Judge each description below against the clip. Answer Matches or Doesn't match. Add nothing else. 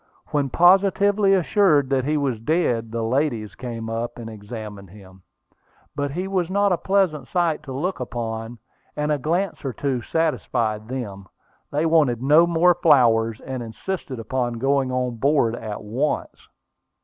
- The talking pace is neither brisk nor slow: Matches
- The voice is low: Matches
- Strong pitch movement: Matches